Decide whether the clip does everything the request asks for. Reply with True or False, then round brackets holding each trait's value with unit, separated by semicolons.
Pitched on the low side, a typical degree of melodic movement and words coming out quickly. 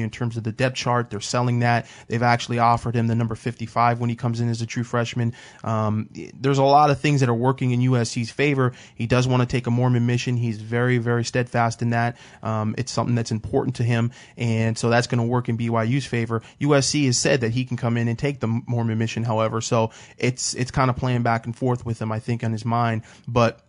False (120 Hz; 1.5 semitones; 245 wpm)